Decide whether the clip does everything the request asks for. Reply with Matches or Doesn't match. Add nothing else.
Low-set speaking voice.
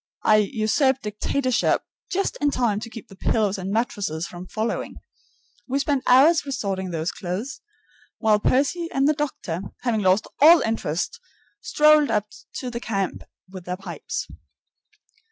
Doesn't match